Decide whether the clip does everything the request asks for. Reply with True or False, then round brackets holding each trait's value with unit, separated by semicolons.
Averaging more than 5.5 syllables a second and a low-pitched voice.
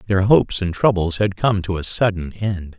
False (5.0 syllables/s; 95 Hz)